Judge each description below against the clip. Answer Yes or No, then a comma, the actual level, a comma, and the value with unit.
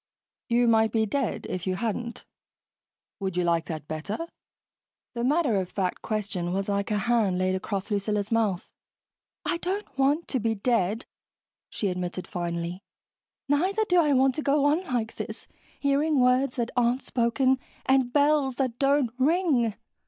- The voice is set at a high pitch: Yes, high, 235 Hz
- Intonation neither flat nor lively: No, wide, 5.8 semitones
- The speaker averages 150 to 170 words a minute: Yes, average, 160 wpm